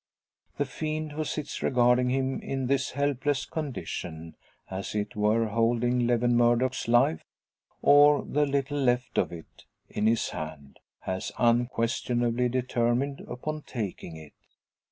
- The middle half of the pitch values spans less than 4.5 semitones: Yes, average, 3.2 semitones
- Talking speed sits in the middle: No, slow, 130 wpm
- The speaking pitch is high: No, low, 125 Hz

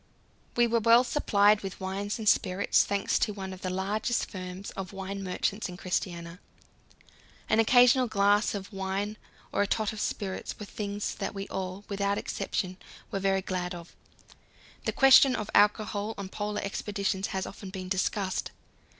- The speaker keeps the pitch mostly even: Yes, narrow, 1.9 semitones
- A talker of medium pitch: No, high, 200 Hz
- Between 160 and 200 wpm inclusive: Yes, average, 165 wpm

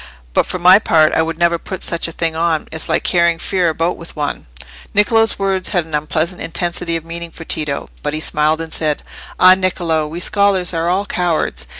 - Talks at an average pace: No, fast, 210 wpm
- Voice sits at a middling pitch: Yes, medium, 170 Hz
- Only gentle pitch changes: Yes, narrow, 2.2 semitones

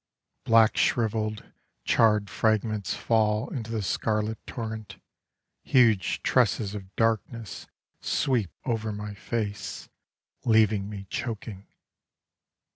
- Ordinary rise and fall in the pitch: No, narrow, 1.6 semitones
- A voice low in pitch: Yes, low, 110 Hz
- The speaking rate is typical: No, slow, 95 wpm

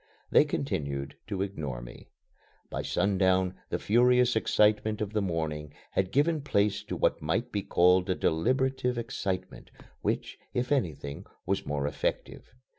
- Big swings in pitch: Yes, wide, 6.8 semitones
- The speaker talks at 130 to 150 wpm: Yes, average, 140 wpm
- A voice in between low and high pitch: No, very low, 95 Hz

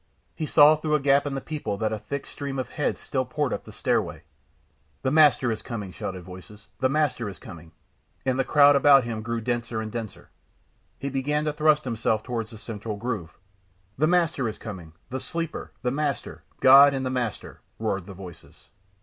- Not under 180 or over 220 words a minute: Yes, average, 195 wpm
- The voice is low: Yes, low, 125 Hz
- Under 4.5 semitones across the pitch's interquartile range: No, average, 4.8 semitones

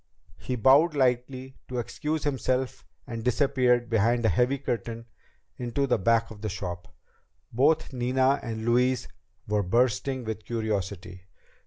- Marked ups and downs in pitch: No, average, 2.9 semitones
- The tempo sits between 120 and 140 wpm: Yes, slow, 135 wpm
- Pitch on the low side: Yes, low, 120 Hz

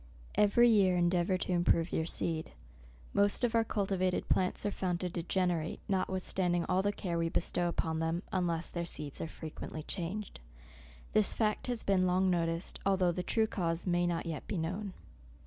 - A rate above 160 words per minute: Yes, average, 180 wpm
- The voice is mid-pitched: Yes, medium, 180 Hz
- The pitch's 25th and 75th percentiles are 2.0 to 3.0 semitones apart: Yes, narrow, 2.5 semitones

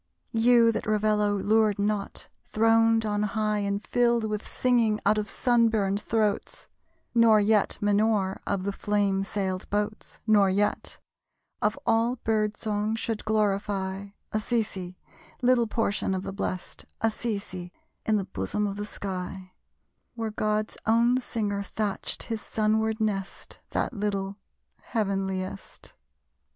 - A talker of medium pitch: No, high, 210 Hz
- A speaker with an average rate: No, slow, 130 wpm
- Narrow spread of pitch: Yes, narrow, 1.9 semitones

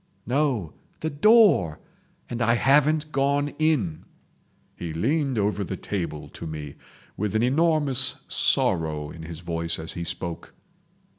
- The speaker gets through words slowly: Yes, slow, 130 wpm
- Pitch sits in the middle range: No, low, 110 Hz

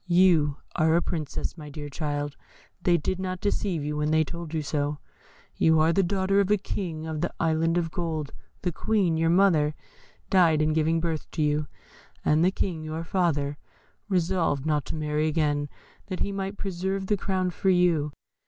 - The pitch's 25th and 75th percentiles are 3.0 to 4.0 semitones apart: Yes, average, 3.3 semitones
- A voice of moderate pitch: Yes, medium, 165 Hz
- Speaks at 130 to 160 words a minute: No, average, 185 wpm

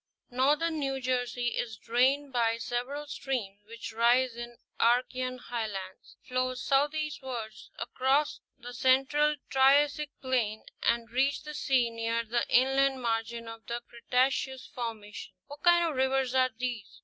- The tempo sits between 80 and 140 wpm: Yes, slow, 135 wpm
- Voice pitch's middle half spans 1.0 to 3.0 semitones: Yes, narrow, 2.6 semitones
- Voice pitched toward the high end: Yes, very high, 255 Hz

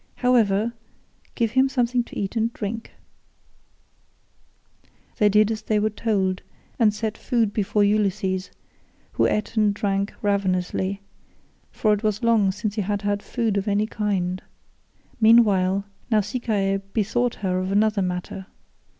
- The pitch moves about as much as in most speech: No, narrow, 2.2 semitones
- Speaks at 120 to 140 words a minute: Yes, slow, 135 wpm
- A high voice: Yes, high, 210 Hz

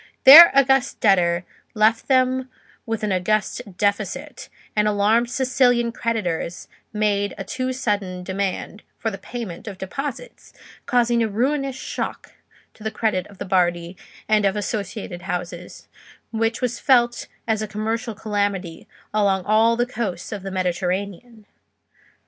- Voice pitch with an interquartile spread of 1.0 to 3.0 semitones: No, average, 3.7 semitones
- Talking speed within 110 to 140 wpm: Yes, slow, 135 wpm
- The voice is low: No, high, 215 Hz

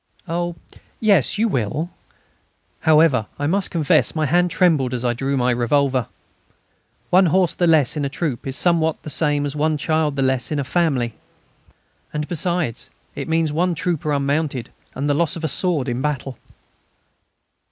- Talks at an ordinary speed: Yes, average, 170 wpm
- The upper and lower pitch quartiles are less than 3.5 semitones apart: No, average, 3.8 semitones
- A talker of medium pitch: Yes, medium, 150 Hz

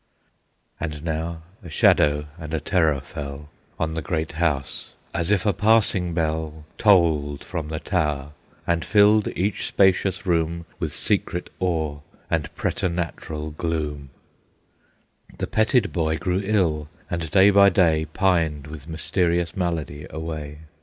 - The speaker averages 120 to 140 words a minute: Yes, slow, 135 wpm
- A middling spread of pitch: Yes, average, 3.1 semitones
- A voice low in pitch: Yes, very low, 80 Hz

